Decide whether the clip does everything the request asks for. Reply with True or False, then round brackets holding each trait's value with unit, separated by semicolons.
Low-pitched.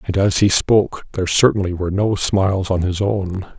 True (95 Hz)